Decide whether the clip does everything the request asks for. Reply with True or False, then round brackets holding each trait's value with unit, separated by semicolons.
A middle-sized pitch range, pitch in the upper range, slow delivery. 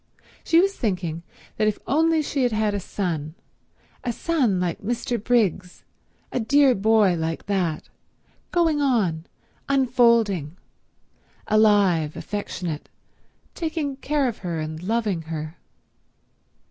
False (6.7 semitones; 210 Hz; 115 wpm)